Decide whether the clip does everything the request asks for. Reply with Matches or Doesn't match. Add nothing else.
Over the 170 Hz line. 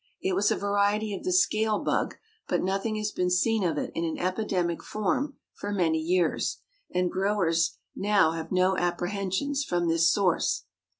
Matches